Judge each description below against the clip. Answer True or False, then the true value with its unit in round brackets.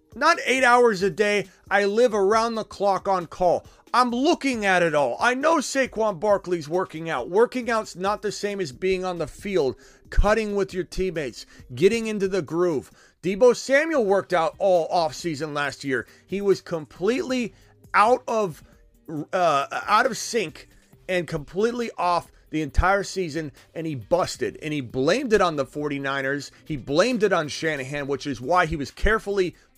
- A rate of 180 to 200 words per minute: False (170 wpm)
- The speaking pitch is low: False (185 Hz)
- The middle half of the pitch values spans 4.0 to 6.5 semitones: True (5.4 semitones)